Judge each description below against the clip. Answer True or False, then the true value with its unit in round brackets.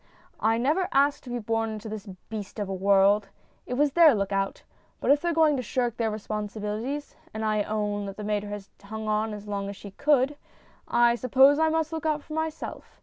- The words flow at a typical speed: False (215 wpm)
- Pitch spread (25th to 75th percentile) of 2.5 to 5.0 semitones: False (5.5 semitones)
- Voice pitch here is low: False (220 Hz)